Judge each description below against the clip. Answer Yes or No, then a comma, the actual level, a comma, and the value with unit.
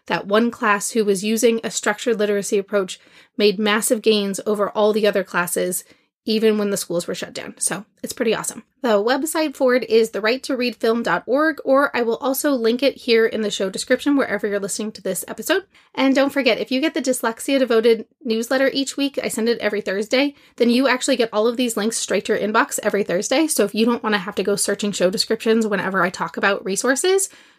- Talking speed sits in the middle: No, fast, 220 wpm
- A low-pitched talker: No, high, 225 Hz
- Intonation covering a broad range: No, average, 3.8 semitones